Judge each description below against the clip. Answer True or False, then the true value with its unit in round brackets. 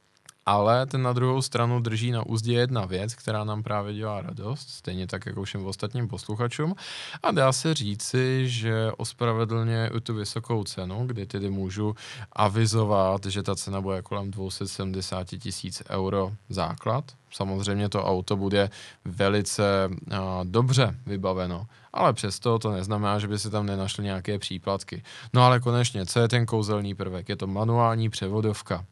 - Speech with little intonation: False (3.1 semitones)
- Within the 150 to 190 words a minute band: True (155 wpm)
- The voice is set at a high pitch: False (105 Hz)